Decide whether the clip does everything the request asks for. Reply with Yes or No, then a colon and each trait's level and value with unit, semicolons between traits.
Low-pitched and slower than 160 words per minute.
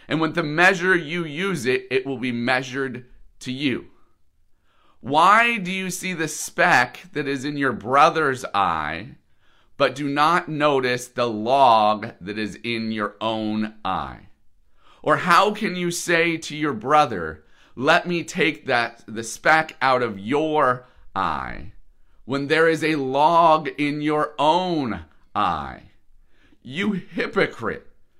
No: medium, 145 Hz; average, 140 wpm